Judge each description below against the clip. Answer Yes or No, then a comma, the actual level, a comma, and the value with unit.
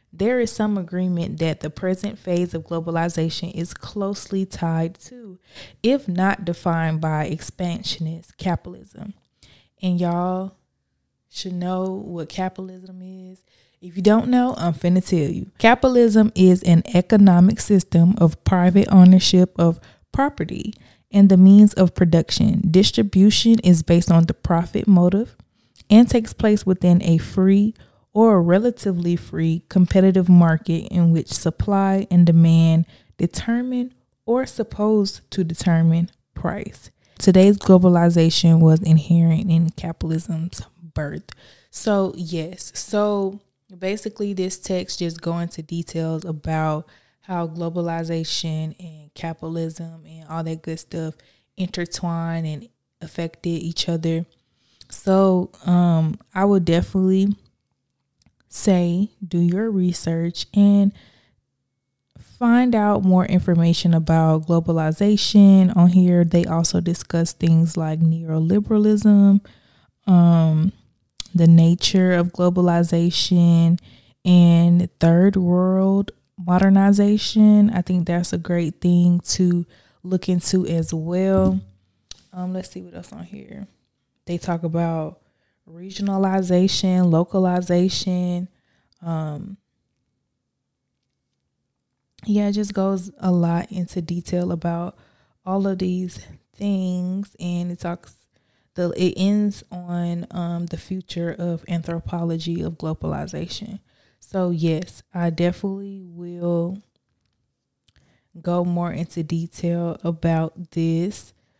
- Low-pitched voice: No, medium, 175 Hz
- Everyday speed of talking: No, slow, 110 wpm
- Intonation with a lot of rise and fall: No, narrow, 2.5 semitones